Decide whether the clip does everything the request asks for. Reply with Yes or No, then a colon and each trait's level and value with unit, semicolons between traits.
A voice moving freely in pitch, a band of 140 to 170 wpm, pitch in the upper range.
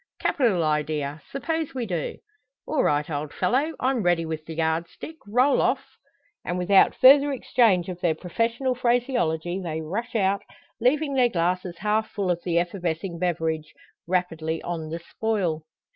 No: wide, 6.6 semitones; average, 155 wpm; medium, 180 Hz